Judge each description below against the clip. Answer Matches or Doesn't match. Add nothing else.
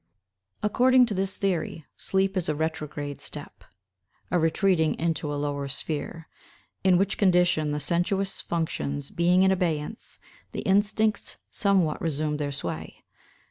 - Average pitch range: Matches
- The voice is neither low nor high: Matches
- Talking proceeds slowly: Matches